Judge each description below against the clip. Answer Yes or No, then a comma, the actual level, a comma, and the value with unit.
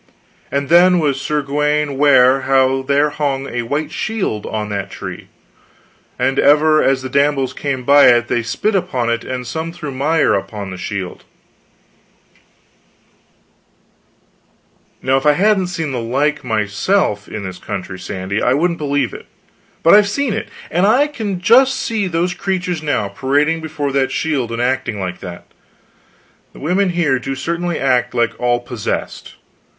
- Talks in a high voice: No, medium, 140 Hz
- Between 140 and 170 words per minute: Yes, average, 160 wpm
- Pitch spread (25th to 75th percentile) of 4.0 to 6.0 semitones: Yes, average, 5.3 semitones